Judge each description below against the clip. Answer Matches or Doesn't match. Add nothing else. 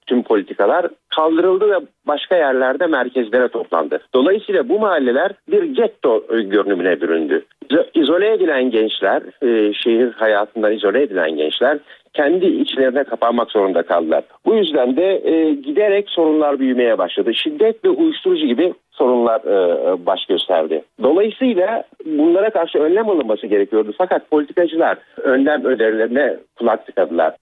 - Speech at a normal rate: Matches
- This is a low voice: Doesn't match